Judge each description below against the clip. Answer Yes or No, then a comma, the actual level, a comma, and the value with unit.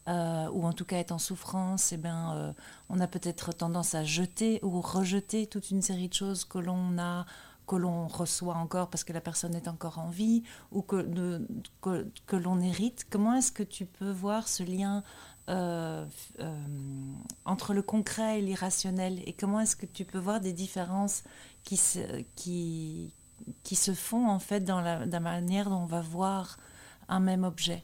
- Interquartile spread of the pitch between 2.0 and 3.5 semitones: Yes, narrow, 2.4 semitones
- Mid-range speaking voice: Yes, medium, 180 Hz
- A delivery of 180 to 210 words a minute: Yes, average, 195 wpm